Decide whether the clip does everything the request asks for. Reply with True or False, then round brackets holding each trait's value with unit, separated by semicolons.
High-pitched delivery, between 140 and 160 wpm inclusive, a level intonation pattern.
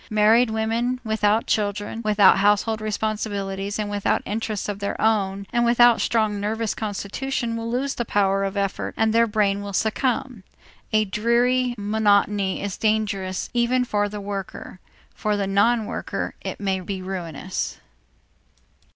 True (210 Hz; 150 wpm; 2.1 semitones)